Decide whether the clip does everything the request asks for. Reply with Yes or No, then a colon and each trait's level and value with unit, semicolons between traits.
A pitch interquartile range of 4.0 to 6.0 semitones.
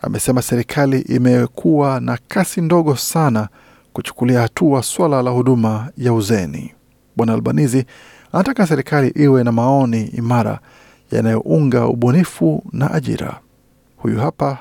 No: average, 3.4 semitones